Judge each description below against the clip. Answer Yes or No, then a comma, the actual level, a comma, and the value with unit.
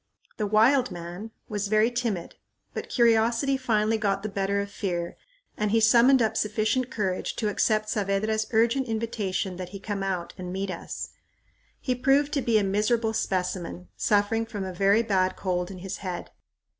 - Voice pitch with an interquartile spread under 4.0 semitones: Yes, average, 2.9 semitones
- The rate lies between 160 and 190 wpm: Yes, average, 170 wpm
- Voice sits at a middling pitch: No, high, 210 Hz